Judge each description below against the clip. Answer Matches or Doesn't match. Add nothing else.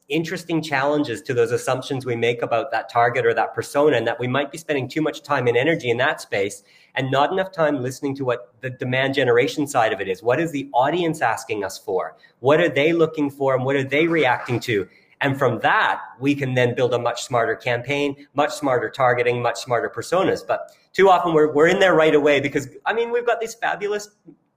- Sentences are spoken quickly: Matches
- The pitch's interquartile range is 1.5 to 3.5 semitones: Doesn't match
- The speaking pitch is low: Doesn't match